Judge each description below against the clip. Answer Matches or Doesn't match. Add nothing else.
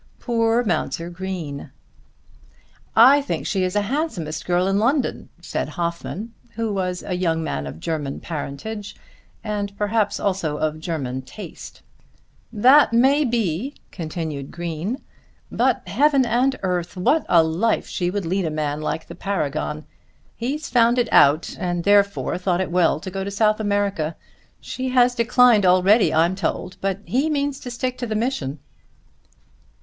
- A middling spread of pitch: Doesn't match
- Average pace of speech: Matches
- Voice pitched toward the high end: Matches